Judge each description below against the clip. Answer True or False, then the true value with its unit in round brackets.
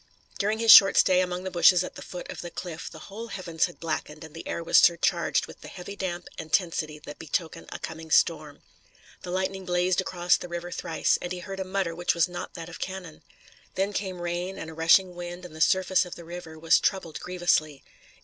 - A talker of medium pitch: True (175 Hz)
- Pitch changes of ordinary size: False (2.2 semitones)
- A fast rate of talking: True (225 wpm)